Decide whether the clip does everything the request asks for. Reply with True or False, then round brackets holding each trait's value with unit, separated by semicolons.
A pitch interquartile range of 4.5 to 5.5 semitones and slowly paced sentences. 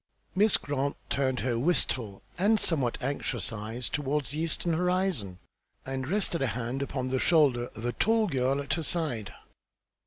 False (5.2 semitones; 160 wpm)